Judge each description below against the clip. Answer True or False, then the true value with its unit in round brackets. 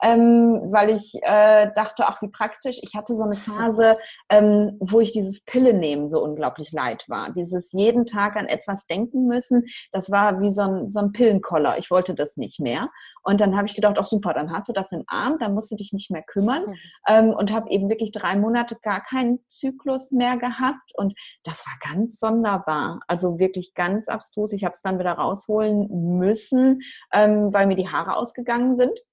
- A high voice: True (210 Hz)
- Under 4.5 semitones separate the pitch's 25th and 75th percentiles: True (2.9 semitones)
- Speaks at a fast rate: True (200 wpm)